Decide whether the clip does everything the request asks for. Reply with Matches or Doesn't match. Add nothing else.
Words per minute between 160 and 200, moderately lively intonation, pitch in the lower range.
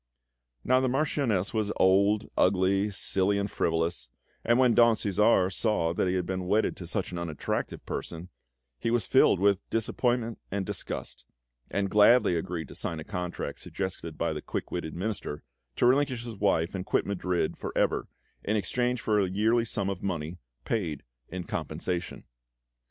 Matches